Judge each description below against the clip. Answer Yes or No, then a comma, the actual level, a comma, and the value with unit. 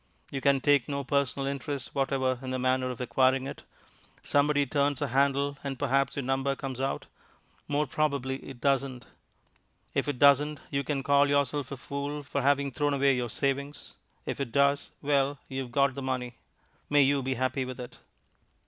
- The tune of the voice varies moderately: No, narrow, 1.4 semitones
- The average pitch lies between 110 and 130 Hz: No, medium, 140 Hz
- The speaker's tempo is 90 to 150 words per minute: No, average, 185 wpm